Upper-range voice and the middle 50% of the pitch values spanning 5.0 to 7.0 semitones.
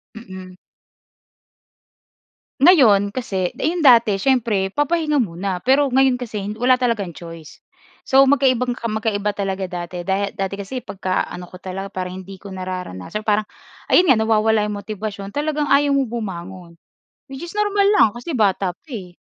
Yes: high, 210 Hz; average, 5.3 semitones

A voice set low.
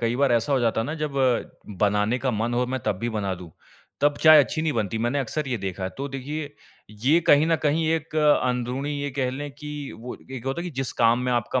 Yes: low, 130 Hz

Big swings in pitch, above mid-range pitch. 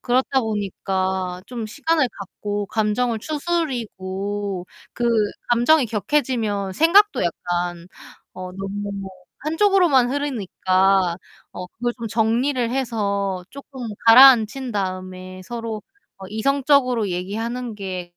No: average, 5.0 semitones; high, 220 Hz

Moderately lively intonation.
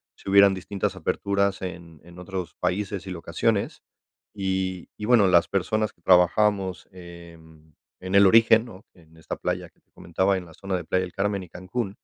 No: narrow, 2.3 semitones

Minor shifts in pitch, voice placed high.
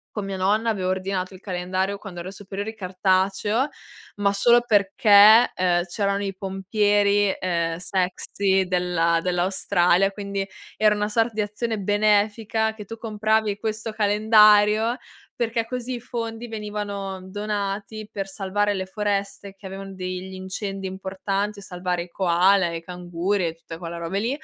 Yes: narrow, 2.1 semitones; high, 200 Hz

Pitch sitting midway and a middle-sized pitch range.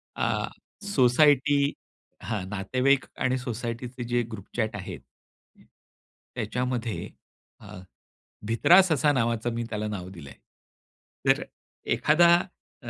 No: low, 120 Hz; average, 4.0 semitones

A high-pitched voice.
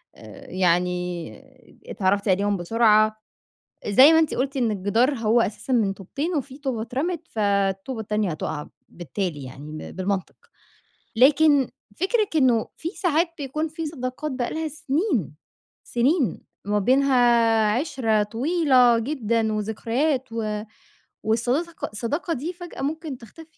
Yes: high, 240 Hz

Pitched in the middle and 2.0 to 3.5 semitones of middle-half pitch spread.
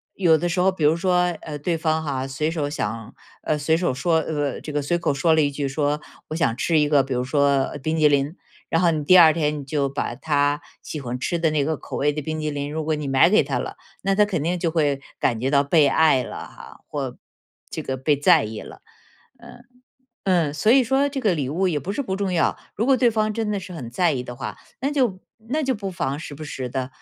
No: medium, 155 Hz; average, 4.0 semitones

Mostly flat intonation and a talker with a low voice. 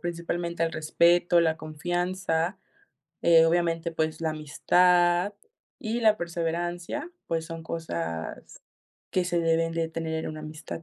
No: narrow, 1.4 semitones; medium, 165 Hz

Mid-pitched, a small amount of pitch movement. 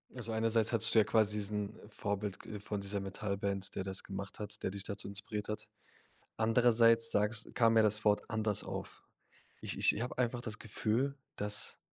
No: low, 105 Hz; narrow, 1.9 semitones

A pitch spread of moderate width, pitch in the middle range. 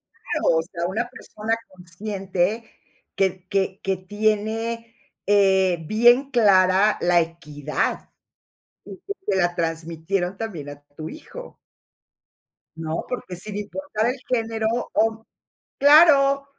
No: average, 4.3 semitones; high, 200 Hz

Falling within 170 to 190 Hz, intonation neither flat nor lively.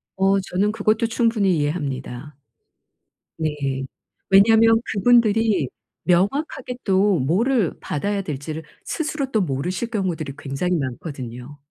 No: medium, 185 Hz; wide, 7.1 semitones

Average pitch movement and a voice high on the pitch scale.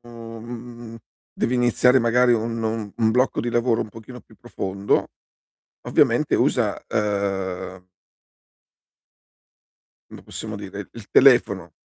No: average, 3.0 semitones; low, 115 Hz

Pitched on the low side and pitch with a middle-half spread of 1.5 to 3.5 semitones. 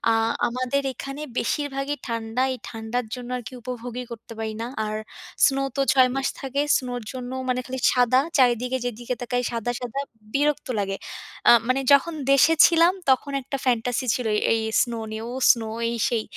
No: very high, 250 Hz; narrow, 2.6 semitones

